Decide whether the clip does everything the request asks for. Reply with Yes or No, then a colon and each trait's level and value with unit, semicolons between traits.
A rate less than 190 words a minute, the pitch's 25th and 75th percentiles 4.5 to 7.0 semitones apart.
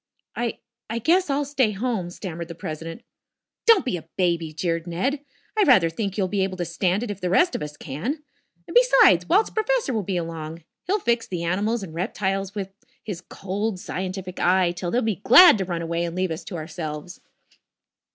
No: average, 200 wpm; wide, 5.4 semitones